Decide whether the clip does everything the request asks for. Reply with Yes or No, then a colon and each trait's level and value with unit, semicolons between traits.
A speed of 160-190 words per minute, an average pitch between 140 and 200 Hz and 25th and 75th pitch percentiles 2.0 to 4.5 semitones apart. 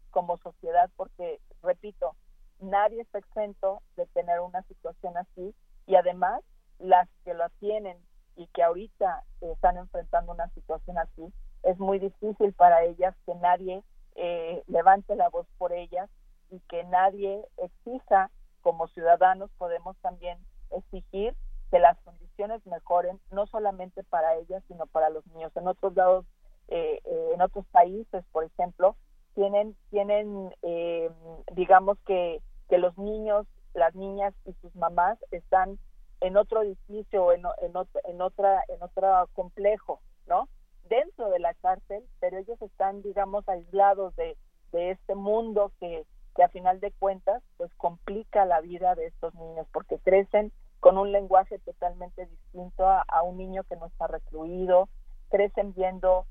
No: average, 150 wpm; medium, 185 Hz; narrow, 2.5 semitones